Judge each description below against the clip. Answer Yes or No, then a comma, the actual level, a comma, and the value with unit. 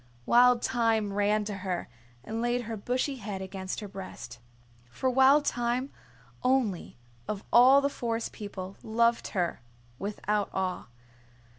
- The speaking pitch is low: No, high, 220 Hz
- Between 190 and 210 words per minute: No, slow, 135 wpm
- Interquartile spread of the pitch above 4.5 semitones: No, average, 3.7 semitones